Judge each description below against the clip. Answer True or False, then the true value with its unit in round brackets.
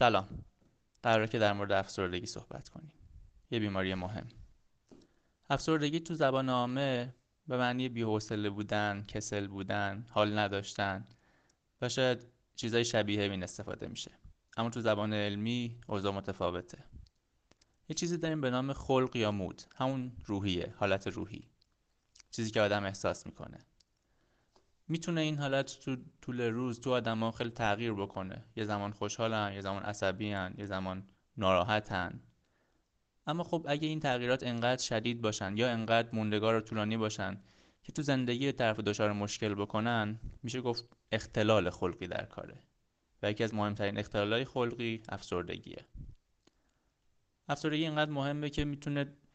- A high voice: False (110 Hz)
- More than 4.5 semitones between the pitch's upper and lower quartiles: False (3.7 semitones)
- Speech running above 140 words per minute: False (135 wpm)